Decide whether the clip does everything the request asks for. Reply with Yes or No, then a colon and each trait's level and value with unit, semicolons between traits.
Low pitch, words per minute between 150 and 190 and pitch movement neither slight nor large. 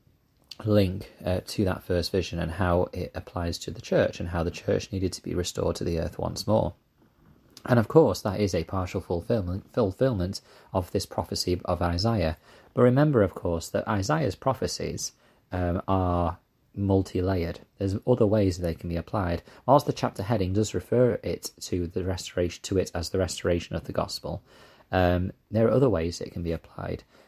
Yes: very low, 95 Hz; average, 185 wpm; average, 3.6 semitones